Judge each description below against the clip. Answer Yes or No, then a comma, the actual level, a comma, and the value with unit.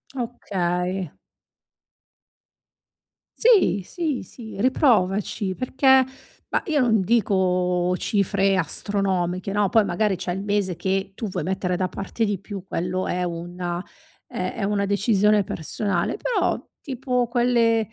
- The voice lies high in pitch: Yes, high, 195 Hz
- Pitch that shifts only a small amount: No, average, 3.9 semitones